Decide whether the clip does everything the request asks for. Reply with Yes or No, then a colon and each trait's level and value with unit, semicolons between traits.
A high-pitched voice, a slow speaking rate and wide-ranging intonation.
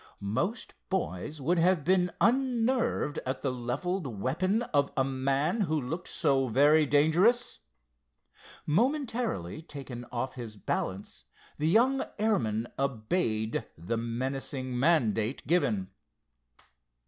No: medium, 145 Hz; slow, 110 wpm; wide, 7.1 semitones